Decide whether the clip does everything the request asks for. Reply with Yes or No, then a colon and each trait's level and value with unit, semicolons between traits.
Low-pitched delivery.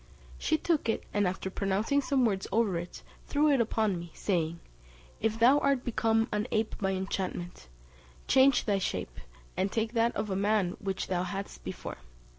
No: high, 210 Hz